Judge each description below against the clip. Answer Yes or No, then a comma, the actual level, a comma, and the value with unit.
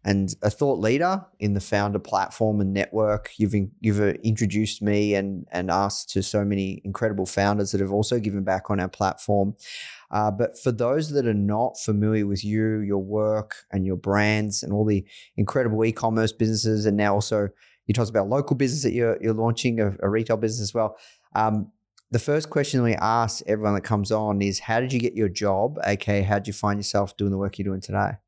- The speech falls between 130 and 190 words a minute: No, fast, 205 wpm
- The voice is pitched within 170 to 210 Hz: No, low, 105 Hz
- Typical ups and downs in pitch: No, narrow, 1.8 semitones